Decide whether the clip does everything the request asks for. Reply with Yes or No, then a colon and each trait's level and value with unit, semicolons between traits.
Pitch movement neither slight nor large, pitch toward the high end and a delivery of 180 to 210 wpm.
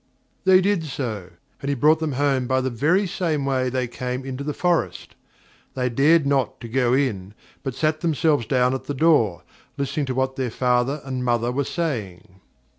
No: average, 3.2 semitones; low, 130 Hz; average, 190 wpm